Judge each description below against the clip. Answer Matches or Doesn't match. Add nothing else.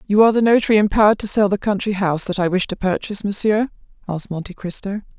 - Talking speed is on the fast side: Matches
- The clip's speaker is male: Doesn't match